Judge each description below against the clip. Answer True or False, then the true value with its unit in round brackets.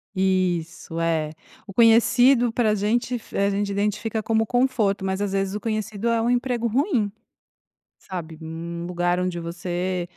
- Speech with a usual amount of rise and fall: True (4.4 semitones)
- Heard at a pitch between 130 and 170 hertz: False (200 Hz)